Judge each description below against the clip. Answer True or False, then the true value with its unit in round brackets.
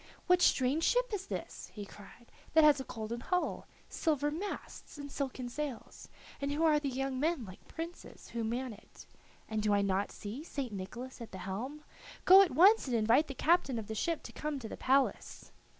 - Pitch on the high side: True (270 Hz)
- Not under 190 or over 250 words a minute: True (200 wpm)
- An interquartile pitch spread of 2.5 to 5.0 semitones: False (5.5 semitones)